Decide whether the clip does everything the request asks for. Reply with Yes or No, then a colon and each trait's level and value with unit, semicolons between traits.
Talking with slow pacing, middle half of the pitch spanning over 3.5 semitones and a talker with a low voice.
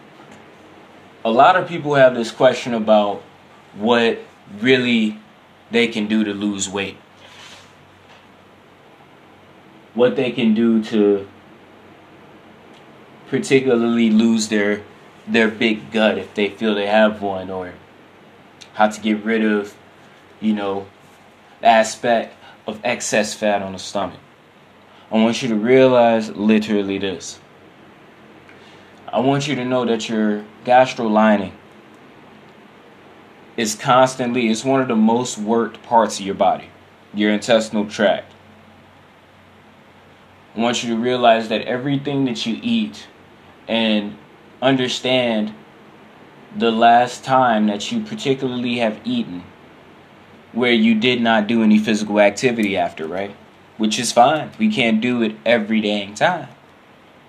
No: slow, 125 wpm; average, 2.7 semitones; low, 110 Hz